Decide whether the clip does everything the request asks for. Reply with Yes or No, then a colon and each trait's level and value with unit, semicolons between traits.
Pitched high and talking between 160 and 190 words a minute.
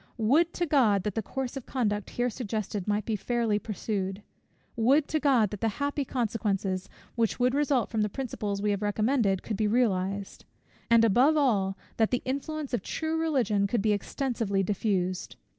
Yes: high, 225 Hz; average, 175 wpm